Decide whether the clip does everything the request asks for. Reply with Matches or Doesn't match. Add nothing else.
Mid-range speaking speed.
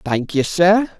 Matches